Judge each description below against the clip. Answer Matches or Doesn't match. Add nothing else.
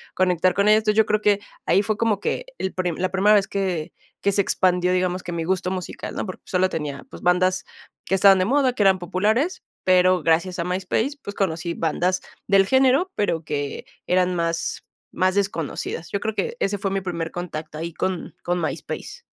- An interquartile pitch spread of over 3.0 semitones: Doesn't match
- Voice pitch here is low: Doesn't match